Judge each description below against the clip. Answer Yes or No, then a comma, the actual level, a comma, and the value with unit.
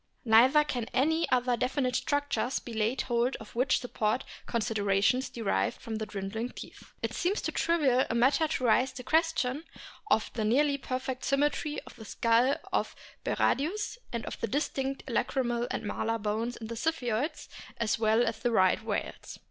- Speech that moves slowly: No, average, 170 wpm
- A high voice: Yes, high, 245 Hz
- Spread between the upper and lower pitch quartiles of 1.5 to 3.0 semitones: No, average, 3.4 semitones